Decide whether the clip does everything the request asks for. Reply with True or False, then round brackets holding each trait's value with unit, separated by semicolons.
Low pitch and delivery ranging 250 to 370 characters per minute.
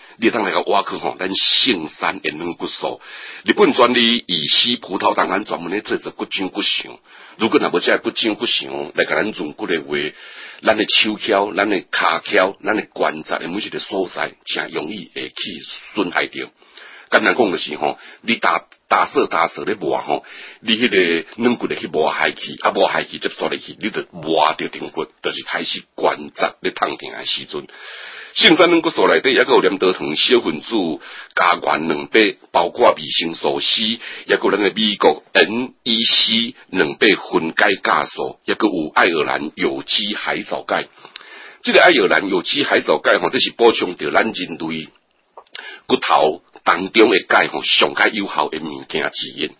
True (115 Hz; 260 characters per minute)